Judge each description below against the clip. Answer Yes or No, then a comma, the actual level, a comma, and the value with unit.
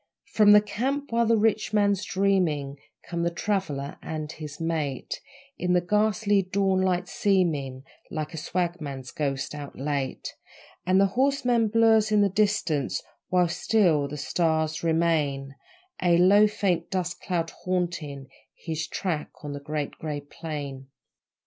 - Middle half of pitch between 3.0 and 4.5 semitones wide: No, average, 5.2 semitones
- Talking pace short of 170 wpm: Yes, average, 140 wpm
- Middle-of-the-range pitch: Yes, medium, 175 Hz